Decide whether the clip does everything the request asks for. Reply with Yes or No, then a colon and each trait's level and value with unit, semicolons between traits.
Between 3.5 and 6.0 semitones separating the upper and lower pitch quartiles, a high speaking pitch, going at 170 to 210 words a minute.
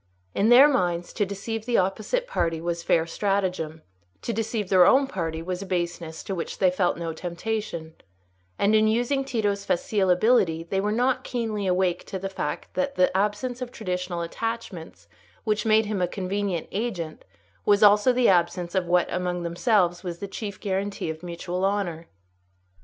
Yes: average, 3.8 semitones; high, 195 Hz; average, 175 wpm